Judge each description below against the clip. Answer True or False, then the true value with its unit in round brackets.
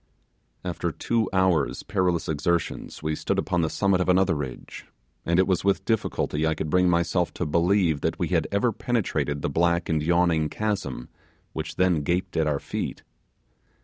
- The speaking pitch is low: True (85 Hz)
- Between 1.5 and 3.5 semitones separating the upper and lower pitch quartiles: True (3.0 semitones)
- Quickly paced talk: False (175 wpm)